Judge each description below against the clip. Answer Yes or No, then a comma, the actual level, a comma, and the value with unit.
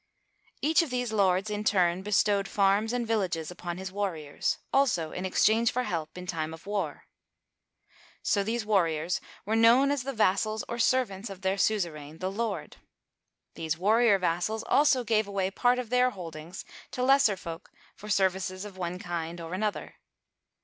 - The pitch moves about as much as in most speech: Yes, average, 4.1 semitones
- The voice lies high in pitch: Yes, high, 200 Hz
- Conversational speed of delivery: Yes, average, 170 wpm